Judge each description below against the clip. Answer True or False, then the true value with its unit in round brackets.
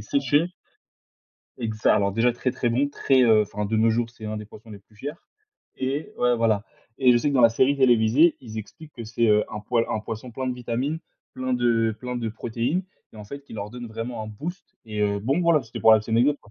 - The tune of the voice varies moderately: True (3.1 semitones)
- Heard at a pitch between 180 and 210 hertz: False (120 Hz)